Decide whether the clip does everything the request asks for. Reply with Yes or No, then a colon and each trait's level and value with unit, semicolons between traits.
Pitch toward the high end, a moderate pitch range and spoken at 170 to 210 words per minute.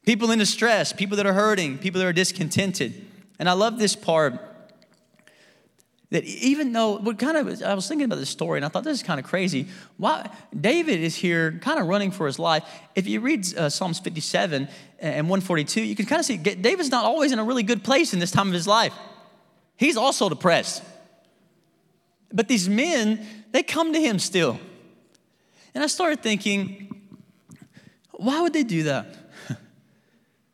Yes: high, 205 Hz; average, 4.7 semitones; average, 185 wpm